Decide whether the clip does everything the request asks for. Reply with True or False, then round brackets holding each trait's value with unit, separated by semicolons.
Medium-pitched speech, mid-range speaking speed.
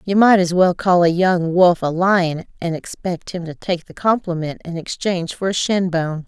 False (175 Hz; 220 wpm)